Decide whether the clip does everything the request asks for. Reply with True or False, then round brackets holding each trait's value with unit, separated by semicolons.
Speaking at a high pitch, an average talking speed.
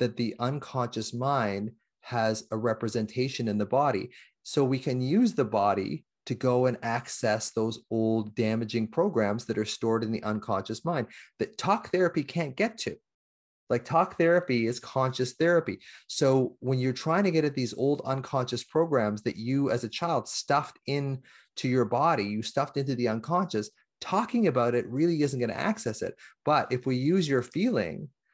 False (125 Hz; 175 wpm)